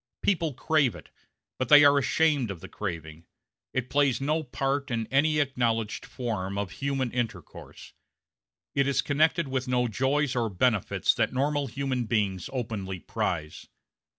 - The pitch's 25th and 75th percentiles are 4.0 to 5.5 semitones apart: Yes, average, 4.4 semitones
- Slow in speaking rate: No, average, 150 wpm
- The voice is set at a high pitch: No, low, 130 Hz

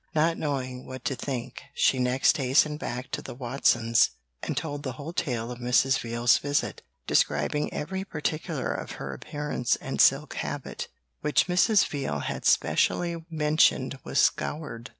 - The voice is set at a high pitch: No, low, 135 Hz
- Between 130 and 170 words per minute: Yes, average, 150 wpm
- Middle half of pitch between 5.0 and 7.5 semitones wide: No, average, 3.6 semitones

